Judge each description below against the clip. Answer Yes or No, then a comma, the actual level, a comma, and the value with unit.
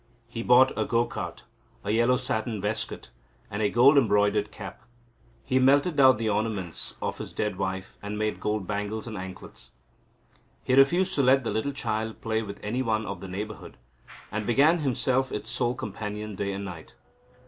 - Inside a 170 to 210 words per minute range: Yes, average, 180 wpm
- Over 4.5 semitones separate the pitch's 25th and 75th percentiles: No, average, 3.8 semitones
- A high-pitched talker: No, low, 110 Hz